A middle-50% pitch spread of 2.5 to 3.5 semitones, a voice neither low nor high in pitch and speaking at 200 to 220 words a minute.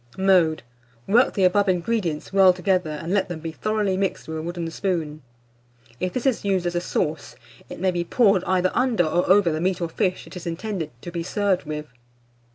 Yes: average, 2.8 semitones; medium, 180 Hz; fast, 205 wpm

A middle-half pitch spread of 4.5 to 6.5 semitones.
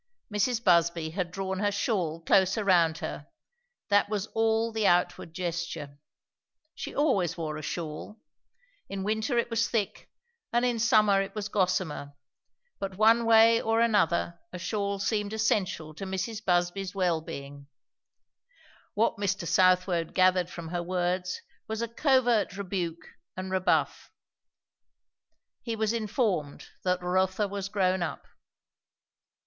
No: average, 3.7 semitones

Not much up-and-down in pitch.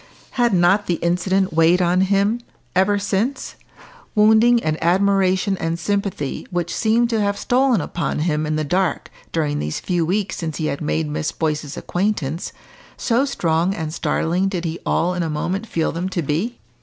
No: average, 3.8 semitones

